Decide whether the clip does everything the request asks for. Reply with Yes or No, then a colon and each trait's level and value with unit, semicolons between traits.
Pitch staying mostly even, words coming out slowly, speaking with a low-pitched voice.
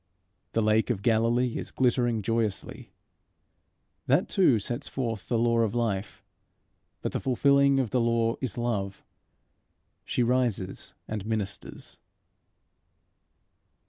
Yes: narrow, 2.2 semitones; slow, 115 wpm; low, 115 Hz